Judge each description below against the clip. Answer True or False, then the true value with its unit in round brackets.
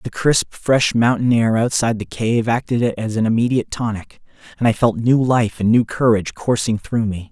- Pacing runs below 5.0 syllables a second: False (5.1 syllables/s)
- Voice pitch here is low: True (115 Hz)